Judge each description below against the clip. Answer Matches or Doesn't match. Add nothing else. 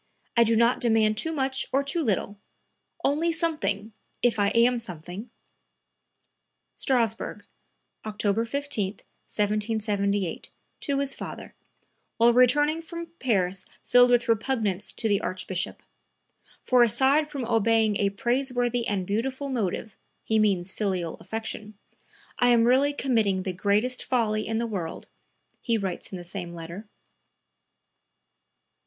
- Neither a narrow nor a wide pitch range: Matches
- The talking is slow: Matches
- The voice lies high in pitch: Matches